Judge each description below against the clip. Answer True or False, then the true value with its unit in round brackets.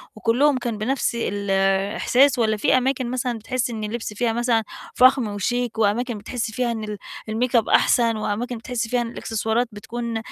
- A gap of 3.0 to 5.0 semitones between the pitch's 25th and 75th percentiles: False (2.4 semitones)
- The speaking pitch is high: True (230 Hz)